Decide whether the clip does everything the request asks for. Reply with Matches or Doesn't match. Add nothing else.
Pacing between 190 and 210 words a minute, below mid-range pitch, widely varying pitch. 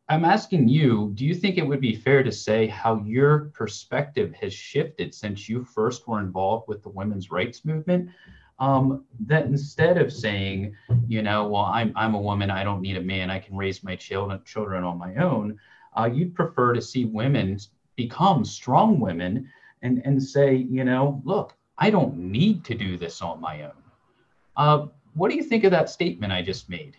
Matches